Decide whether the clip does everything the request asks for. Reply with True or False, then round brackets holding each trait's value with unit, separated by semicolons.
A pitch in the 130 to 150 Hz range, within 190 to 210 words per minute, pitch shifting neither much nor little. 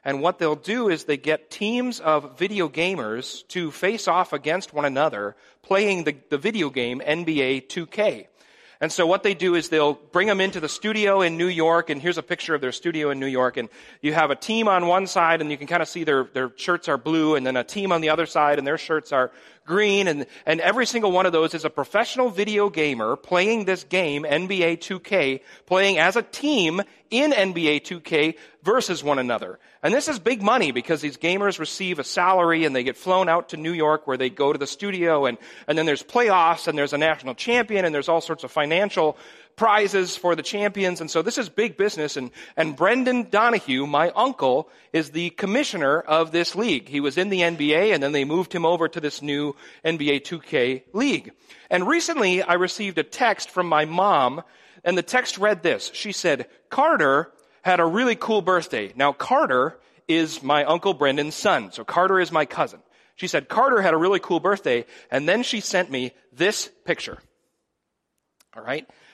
False (170 Hz; 205 wpm; 4.7 semitones)